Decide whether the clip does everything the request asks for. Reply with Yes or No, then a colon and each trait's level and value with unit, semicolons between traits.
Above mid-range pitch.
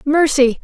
Yes: very high, 280 Hz